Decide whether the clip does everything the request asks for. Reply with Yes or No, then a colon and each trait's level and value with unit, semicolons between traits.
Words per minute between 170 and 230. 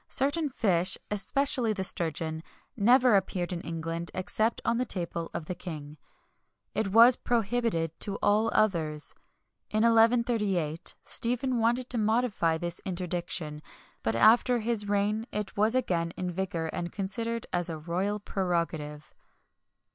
No: slow, 135 wpm